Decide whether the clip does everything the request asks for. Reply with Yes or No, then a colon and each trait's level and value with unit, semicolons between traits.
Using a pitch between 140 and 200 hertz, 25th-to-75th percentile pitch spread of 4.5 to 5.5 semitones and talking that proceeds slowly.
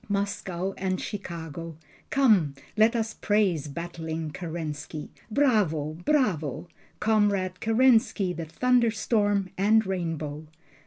Yes: high, 190 Hz; average, 5.0 semitones; slow, 95 wpm